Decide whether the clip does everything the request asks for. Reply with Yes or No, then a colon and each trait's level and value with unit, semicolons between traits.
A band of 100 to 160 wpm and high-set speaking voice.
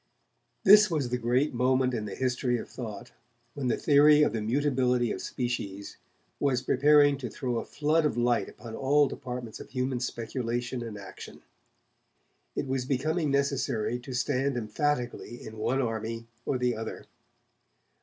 No: average, 155 wpm; low, 125 Hz